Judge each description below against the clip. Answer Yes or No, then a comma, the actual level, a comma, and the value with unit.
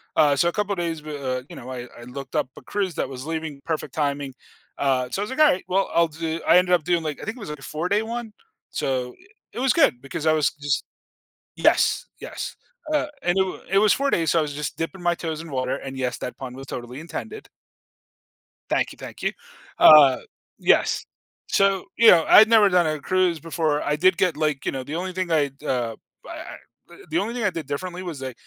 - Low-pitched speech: No, medium, 160 Hz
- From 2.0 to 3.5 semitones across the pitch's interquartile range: No, average, 5.0 semitones